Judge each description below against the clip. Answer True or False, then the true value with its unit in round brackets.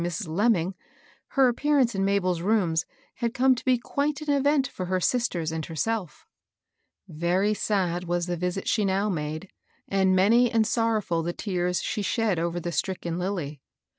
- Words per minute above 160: True (170 wpm)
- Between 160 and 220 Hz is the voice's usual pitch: True (190 Hz)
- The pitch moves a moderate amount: True (4.8 semitones)